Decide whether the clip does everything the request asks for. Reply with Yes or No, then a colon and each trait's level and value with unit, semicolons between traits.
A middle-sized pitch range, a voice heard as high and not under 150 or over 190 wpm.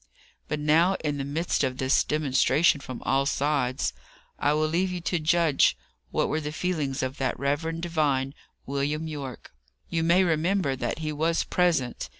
No: average, 3.2 semitones; medium, 150 Hz; average, 165 wpm